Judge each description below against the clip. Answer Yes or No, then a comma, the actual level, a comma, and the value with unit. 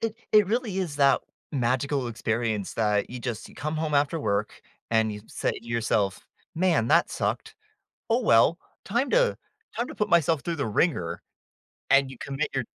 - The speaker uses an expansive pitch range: Yes, wide, 6.9 semitones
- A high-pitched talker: No, medium, 140 Hz